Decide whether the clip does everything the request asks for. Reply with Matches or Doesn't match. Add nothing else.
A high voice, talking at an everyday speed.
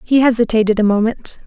Matches